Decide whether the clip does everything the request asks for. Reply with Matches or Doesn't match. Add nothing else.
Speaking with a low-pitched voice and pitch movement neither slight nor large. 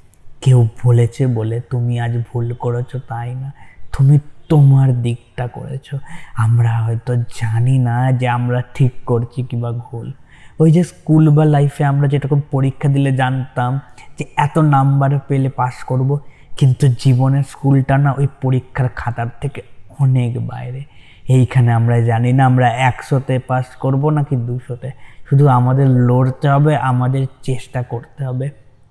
Doesn't match